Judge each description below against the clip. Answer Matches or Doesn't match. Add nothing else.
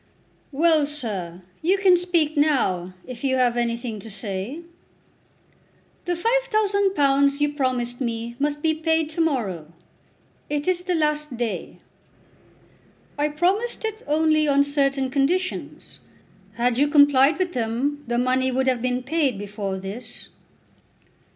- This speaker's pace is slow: Matches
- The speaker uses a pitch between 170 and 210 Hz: Doesn't match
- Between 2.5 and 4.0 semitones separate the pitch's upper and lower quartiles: Doesn't match